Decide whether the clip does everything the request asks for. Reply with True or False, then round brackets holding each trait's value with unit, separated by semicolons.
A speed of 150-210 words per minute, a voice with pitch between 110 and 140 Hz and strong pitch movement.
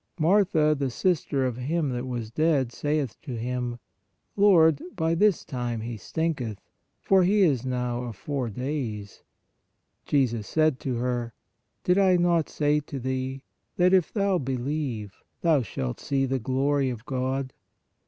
False (155 wpm; 135 Hz; 4.5 semitones)